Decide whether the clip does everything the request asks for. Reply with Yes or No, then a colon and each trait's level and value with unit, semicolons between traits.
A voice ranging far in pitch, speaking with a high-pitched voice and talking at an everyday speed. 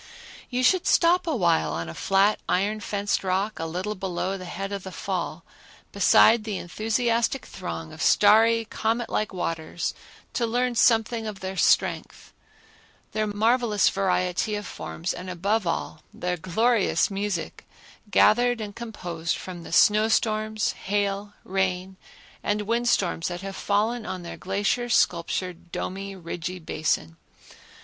No: average, 3.5 semitones; high, 200 Hz; average, 145 wpm